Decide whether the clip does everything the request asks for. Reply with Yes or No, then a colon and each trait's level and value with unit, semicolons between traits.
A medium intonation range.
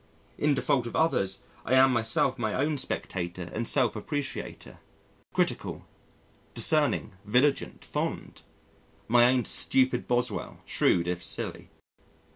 Yes: average, 3.9 semitones